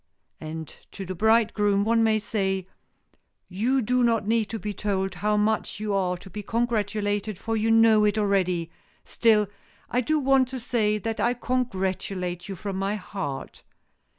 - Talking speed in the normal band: Yes, average, 160 wpm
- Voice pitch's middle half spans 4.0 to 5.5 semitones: No, average, 2.8 semitones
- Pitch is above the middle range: Yes, high, 210 Hz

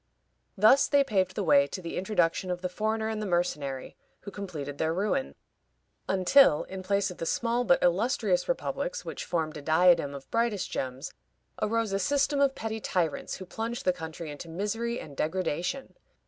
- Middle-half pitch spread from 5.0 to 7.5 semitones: Yes, average, 5.3 semitones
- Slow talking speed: No, average, 175 wpm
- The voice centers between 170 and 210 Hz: Yes, medium, 185 Hz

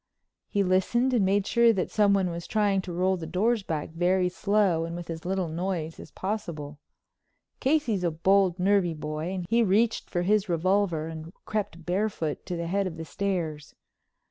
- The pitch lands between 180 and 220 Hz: Yes, medium, 185 Hz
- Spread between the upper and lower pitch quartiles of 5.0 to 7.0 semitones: No, average, 3.3 semitones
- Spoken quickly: No, average, 180 wpm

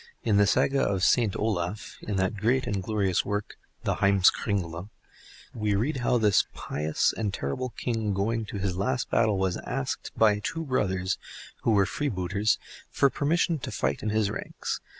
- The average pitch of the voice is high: No, low, 105 Hz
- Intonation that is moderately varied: Yes, average, 3.1 semitones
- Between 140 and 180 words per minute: Yes, average, 170 wpm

